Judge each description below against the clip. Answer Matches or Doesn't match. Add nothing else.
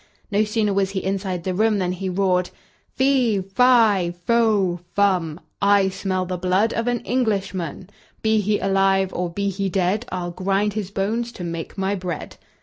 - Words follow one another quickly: Doesn't match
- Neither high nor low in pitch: Doesn't match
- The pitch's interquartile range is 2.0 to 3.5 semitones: Matches